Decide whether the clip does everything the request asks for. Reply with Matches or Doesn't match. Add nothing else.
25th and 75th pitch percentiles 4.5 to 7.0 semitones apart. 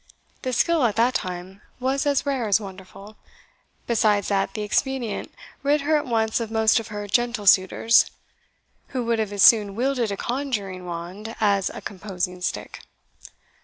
Doesn't match